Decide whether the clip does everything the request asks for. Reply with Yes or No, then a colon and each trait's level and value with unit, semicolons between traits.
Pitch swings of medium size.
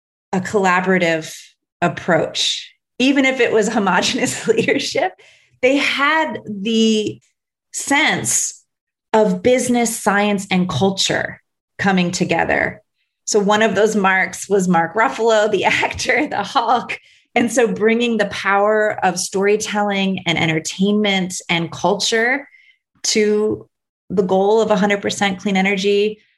Yes: average, 3.1 semitones